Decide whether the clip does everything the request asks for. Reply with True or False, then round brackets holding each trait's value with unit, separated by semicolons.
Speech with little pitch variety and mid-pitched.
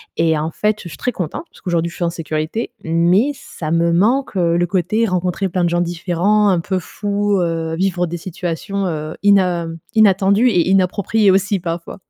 False (3.0 semitones; 180 Hz)